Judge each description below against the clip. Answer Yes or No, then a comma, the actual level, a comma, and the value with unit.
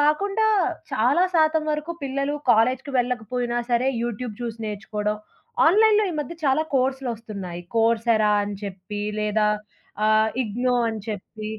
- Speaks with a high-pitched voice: Yes, high, 240 Hz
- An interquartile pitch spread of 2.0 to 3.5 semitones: No, average, 4.5 semitones